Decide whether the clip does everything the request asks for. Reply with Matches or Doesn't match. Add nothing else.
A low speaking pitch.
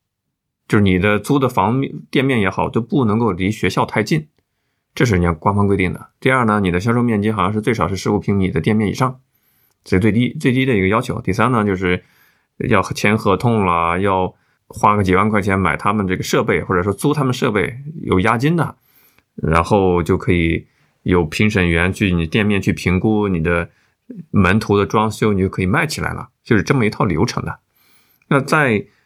Matches